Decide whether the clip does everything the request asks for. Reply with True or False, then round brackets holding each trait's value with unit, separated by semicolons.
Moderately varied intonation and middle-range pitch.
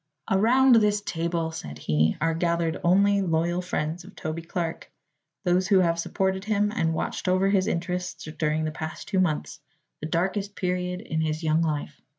True (3.1 semitones; 175 Hz)